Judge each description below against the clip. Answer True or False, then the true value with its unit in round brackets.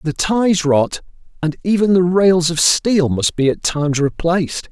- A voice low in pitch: False (170 Hz)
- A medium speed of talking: True (180 wpm)